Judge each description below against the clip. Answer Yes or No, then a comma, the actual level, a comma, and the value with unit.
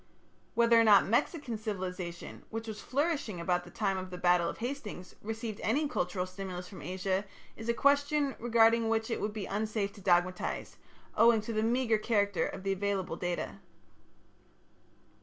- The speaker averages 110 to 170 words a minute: Yes, average, 165 wpm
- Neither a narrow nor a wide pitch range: Yes, average, 3.7 semitones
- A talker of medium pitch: No, high, 210 Hz